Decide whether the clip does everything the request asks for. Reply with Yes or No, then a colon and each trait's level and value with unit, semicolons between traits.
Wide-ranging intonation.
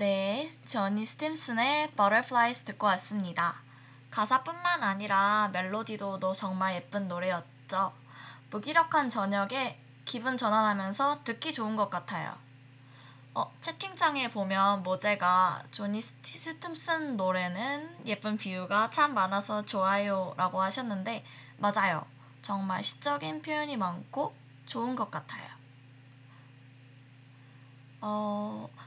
Yes: wide, 8.3 semitones